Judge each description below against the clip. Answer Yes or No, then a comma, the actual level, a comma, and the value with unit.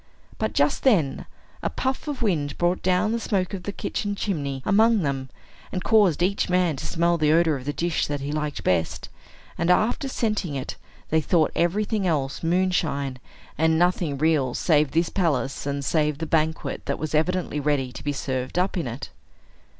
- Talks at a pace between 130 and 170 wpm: No, average, 185 wpm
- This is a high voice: No, medium, 160 Hz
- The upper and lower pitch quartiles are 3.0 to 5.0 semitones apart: Yes, average, 4.3 semitones